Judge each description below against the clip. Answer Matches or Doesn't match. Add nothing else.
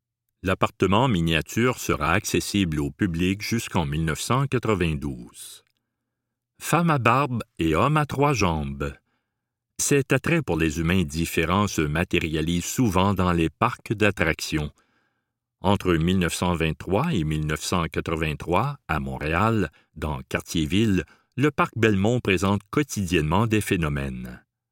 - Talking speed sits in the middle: Doesn't match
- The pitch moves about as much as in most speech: Doesn't match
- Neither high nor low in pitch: Doesn't match